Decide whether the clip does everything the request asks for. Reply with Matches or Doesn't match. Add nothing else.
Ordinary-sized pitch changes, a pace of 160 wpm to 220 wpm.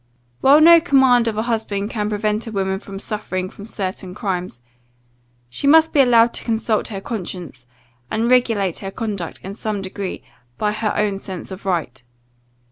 Matches